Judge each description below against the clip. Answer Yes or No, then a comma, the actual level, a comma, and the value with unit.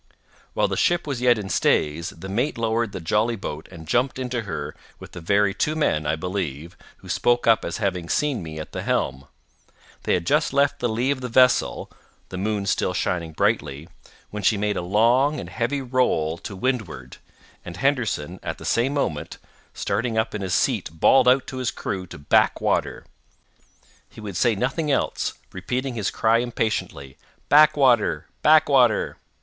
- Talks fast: No, average, 180 wpm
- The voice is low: Yes, low, 110 Hz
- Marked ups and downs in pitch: Yes, wide, 6.3 semitones